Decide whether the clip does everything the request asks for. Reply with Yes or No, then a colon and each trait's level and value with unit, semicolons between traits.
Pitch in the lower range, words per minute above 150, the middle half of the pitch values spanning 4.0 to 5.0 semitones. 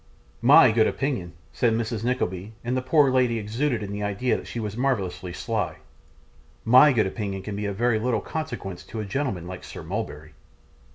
Yes: low, 110 Hz; average, 185 wpm; average, 4.3 semitones